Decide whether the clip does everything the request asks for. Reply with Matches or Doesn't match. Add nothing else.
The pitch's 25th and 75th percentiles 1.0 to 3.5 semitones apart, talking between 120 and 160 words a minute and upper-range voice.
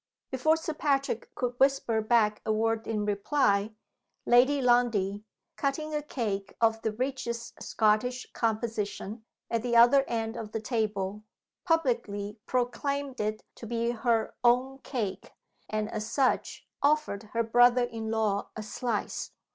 Matches